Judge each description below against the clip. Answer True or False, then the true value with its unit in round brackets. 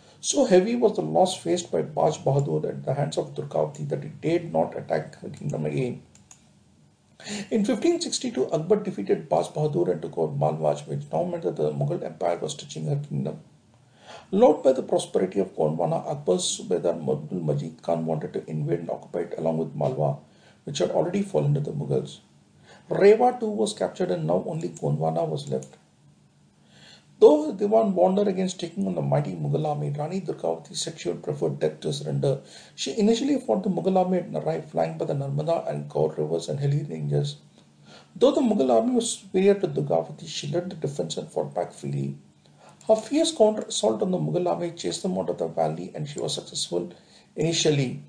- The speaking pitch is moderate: True (155 Hz)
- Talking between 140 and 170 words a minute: False (190 wpm)